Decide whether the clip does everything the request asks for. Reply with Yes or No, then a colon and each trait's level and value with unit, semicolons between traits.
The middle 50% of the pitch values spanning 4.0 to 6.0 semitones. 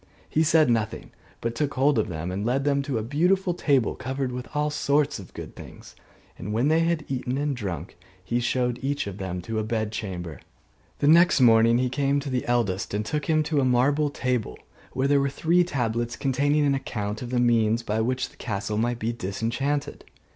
Yes: average, 4.3 semitones